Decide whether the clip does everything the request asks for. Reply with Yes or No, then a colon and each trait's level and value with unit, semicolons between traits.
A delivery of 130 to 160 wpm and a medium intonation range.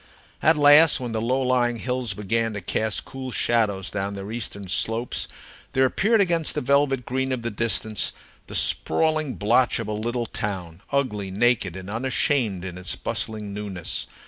No: average, 170 wpm; average, 4.1 semitones